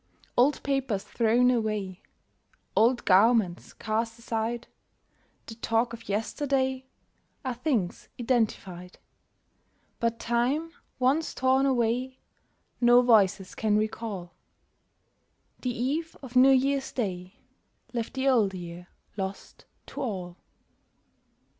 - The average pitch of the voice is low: No, high, 235 Hz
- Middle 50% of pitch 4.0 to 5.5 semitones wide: No, average, 3.6 semitones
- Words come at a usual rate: No, slow, 105 wpm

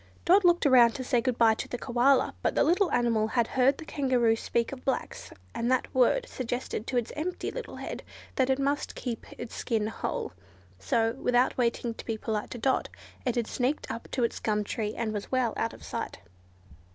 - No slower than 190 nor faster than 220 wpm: Yes, fast, 205 wpm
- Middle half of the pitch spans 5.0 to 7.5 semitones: No, average, 2.7 semitones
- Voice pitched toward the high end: Yes, high, 245 Hz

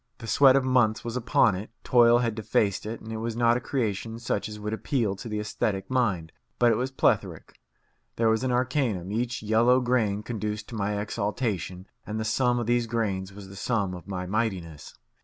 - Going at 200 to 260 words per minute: Yes, fast, 205 wpm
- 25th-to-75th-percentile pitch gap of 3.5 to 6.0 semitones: No, average, 3.0 semitones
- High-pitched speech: No, low, 110 Hz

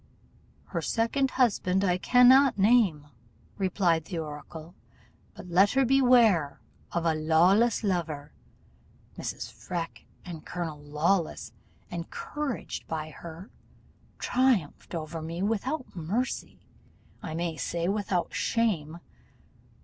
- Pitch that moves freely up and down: Yes, wide, 5.9 semitones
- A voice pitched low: No, medium, 180 Hz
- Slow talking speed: Yes, slow, 105 wpm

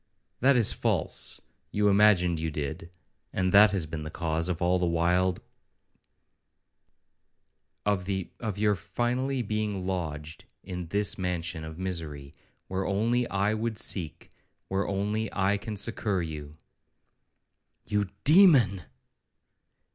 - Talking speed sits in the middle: No, slow, 125 wpm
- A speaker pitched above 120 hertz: No, very low, 95 Hz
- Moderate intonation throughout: Yes, average, 3.9 semitones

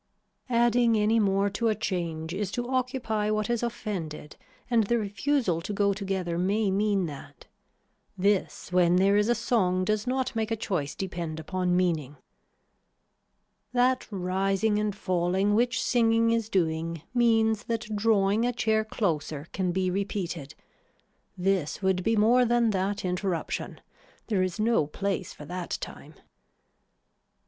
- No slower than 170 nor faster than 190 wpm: No, average, 145 wpm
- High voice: Yes, high, 200 Hz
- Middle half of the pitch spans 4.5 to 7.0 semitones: No, average, 3.8 semitones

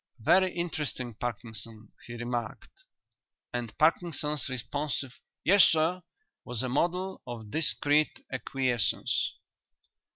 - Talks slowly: Yes, slow, 95 wpm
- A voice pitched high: No, low, 135 Hz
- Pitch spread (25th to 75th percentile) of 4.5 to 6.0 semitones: Yes, average, 5.0 semitones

